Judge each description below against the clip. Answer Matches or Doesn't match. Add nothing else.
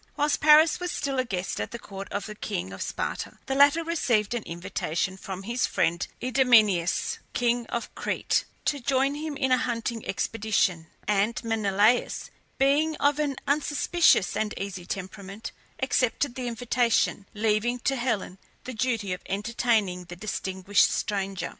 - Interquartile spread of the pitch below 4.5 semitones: Doesn't match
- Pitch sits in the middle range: Doesn't match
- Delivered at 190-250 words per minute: Doesn't match